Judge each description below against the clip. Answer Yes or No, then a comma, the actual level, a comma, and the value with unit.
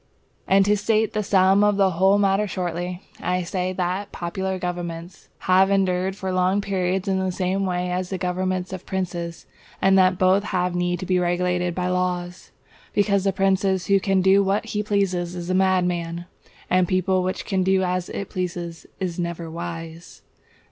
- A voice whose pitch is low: No, medium, 185 Hz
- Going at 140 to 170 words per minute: No, average, 185 wpm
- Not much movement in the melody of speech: Yes, narrow, 1.4 semitones